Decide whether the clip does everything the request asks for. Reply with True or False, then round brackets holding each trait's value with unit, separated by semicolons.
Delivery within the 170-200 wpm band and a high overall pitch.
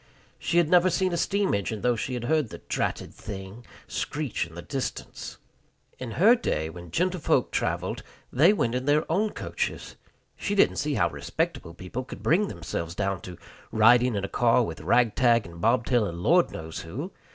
False (185 wpm; 120 Hz)